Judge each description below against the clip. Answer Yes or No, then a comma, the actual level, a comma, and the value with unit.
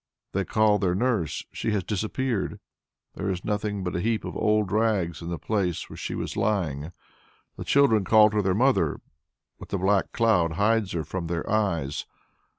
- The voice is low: Yes, low, 100 Hz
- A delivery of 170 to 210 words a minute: Yes, average, 180 wpm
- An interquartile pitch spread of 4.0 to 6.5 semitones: No, average, 3.6 semitones